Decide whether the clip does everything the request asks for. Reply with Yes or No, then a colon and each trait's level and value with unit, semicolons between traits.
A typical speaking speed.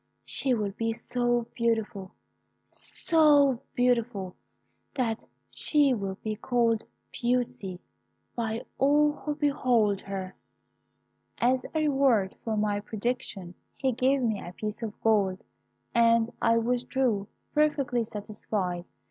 No: slow, 115 wpm